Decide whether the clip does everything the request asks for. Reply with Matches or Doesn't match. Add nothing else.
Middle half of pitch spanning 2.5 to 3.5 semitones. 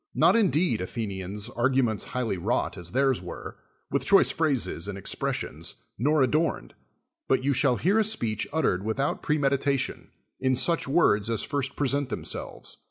Doesn't match